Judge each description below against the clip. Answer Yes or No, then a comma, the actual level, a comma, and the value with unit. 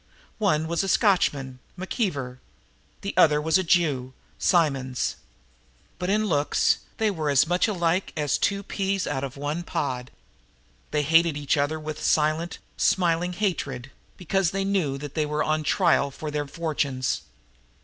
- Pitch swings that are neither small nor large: Yes, average, 4.2 semitones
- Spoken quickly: No, average, 150 wpm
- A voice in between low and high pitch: Yes, medium, 155 Hz